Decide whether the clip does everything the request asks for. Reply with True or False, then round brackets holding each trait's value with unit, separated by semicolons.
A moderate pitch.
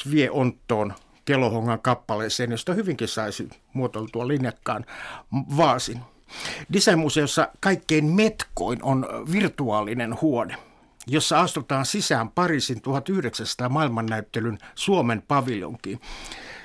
False (130 Hz)